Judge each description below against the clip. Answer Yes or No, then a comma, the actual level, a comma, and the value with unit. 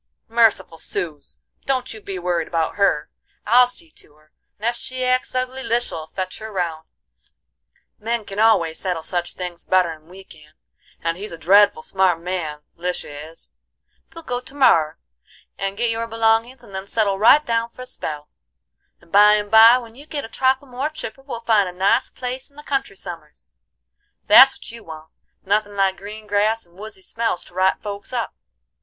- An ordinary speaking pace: Yes, average, 185 wpm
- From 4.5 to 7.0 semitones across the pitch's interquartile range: Yes, average, 5.1 semitones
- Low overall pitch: No, high, 205 Hz